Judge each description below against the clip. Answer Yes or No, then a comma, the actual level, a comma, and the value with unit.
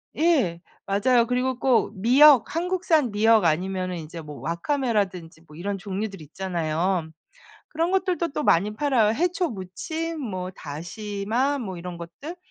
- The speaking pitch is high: Yes, high, 210 Hz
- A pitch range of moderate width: No, wide, 7.7 semitones